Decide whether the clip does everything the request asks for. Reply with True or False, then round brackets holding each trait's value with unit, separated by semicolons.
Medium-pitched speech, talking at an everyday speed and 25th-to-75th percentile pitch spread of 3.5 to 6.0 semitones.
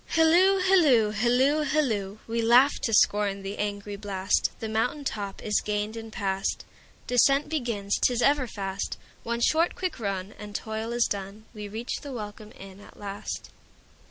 False (220 Hz; 145 wpm; 3.8 semitones)